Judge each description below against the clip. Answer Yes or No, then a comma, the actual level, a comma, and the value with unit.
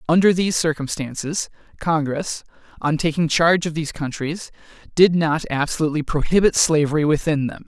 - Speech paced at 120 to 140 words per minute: Yes, slow, 135 wpm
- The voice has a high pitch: No, medium, 160 Hz